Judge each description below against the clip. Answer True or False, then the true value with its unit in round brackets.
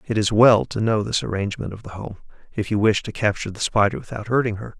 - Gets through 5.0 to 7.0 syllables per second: True (6.4 syllables/s)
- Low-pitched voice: True (105 Hz)